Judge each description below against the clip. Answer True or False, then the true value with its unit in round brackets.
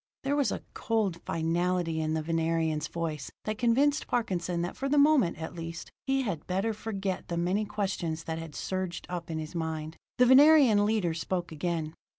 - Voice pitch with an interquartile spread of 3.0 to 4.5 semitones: False (5.1 semitones)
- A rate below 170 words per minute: False (180 wpm)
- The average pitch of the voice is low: False (175 Hz)